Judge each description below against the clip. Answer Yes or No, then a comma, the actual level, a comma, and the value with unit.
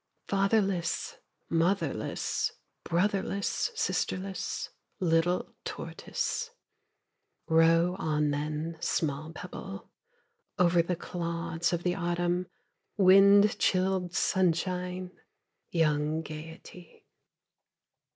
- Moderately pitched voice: Yes, medium, 175 Hz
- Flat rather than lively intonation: Yes, narrow, 2.2 semitones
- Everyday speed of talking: No, slow, 75 wpm